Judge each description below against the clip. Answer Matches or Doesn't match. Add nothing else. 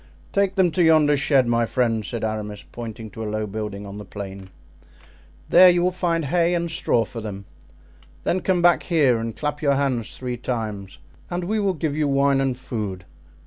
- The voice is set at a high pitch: Doesn't match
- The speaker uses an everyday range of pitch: Doesn't match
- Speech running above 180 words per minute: Matches